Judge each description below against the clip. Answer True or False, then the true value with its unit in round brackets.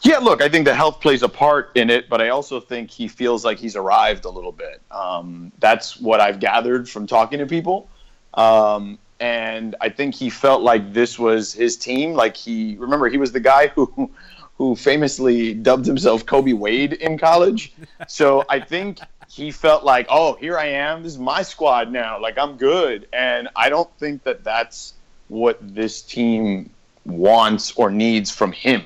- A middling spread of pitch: False (5.7 semitones)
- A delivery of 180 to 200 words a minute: True (190 wpm)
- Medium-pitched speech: False (130 Hz)